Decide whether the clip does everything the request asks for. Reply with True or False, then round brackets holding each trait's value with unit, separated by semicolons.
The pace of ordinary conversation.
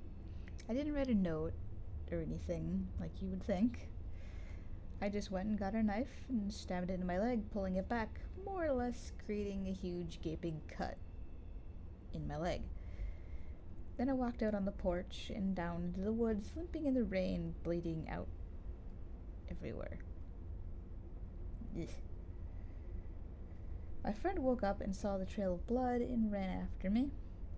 True (155 wpm)